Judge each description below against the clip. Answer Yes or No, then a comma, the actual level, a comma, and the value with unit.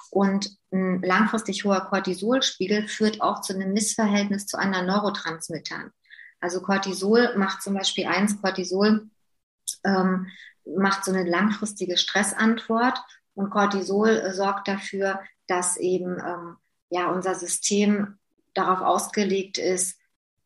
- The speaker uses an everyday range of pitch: No, narrow, 1.8 semitones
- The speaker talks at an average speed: No, slow, 115 wpm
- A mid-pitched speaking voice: No, high, 195 Hz